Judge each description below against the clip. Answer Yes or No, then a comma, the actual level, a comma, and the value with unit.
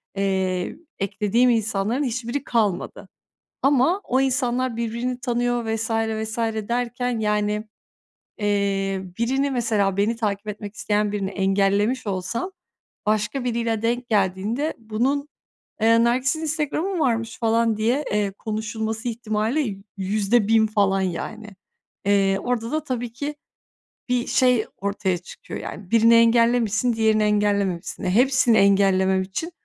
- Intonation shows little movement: No, average, 3.1 semitones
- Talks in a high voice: Yes, high, 220 Hz